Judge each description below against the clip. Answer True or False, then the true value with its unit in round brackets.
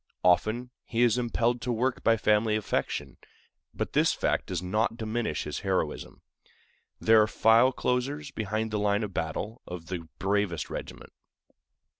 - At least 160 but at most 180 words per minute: False (150 wpm)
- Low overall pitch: True (110 Hz)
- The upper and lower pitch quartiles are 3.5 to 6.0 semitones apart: False (2.9 semitones)